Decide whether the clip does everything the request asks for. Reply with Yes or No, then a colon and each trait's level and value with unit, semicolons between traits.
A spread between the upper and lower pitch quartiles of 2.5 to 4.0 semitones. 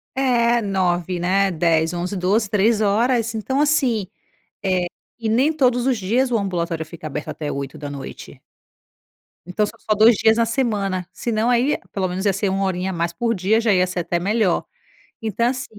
No: average, 4.5 semitones